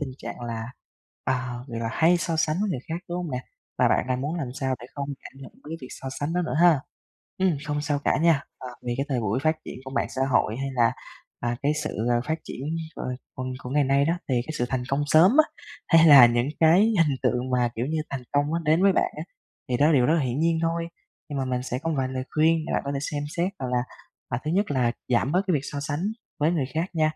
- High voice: No, medium, 145 Hz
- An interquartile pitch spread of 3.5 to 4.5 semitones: Yes, average, 4.1 semitones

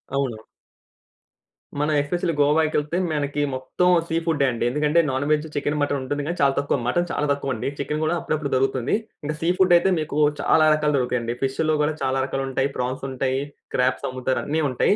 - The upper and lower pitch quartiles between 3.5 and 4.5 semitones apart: No, average, 2.7 semitones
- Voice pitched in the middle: Yes, medium, 145 Hz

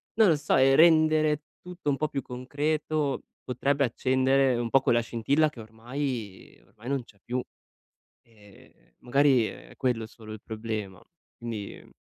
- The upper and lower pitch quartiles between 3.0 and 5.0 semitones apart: Yes, average, 4.2 semitones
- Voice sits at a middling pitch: No, low, 130 Hz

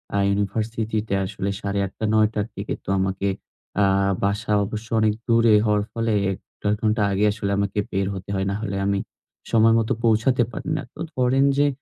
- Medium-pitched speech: No, low, 105 Hz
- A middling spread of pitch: No, narrow, 2.2 semitones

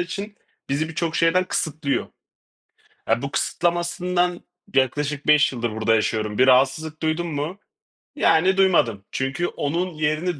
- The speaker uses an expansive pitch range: No, average, 4.5 semitones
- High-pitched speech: No, medium, 155 Hz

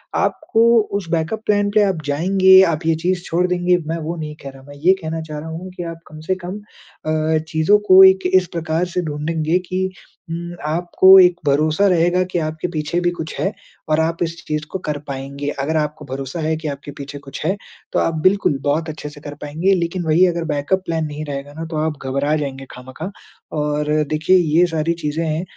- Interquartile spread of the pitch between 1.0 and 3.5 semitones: Yes, average, 3.0 semitones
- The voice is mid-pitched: Yes, medium, 160 Hz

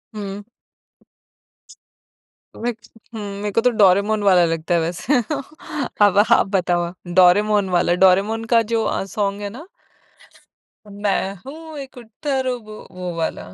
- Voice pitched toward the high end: Yes, high, 205 Hz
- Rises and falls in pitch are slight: No, average, 3.7 semitones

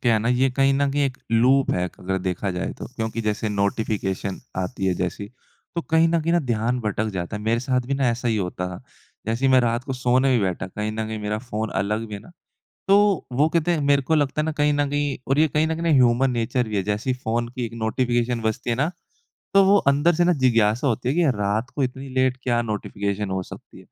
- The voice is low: Yes, low, 120 Hz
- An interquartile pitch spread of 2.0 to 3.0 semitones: No, average, 4.3 semitones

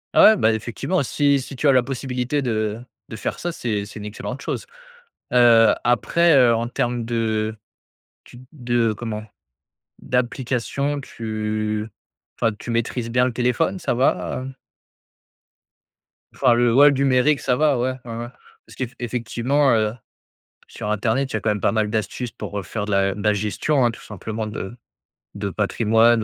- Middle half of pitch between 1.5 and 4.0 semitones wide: Yes, average, 3.0 semitones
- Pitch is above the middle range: No, low, 120 Hz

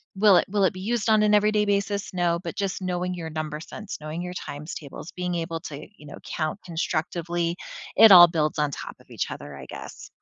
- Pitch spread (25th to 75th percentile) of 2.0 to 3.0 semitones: No, average, 4.1 semitones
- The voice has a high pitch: No, medium, 175 Hz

